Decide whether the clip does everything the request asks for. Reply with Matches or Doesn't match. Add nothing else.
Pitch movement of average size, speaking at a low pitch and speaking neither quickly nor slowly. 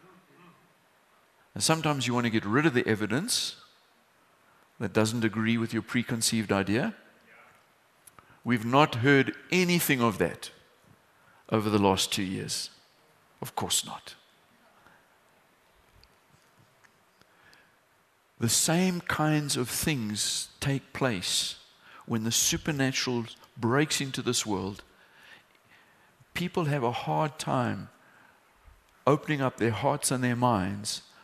Doesn't match